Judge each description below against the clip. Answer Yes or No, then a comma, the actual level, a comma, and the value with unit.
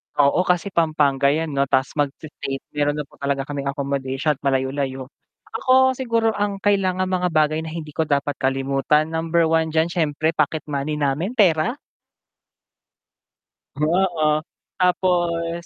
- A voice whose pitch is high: No, medium, 155 Hz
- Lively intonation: No, average, 3.7 semitones